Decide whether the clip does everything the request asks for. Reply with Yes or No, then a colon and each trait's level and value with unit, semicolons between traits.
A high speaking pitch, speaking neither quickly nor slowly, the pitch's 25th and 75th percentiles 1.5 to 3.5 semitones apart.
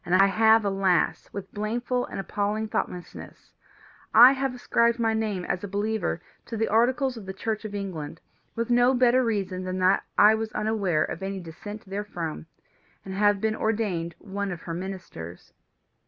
Yes: high, 205 Hz; average, 165 wpm; average, 3.0 semitones